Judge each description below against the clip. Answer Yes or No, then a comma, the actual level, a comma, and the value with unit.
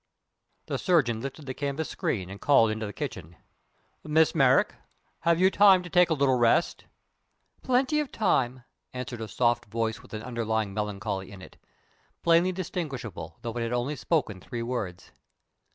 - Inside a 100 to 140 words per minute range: No, average, 165 wpm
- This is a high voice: No, low, 125 Hz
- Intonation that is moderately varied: No, wide, 6.4 semitones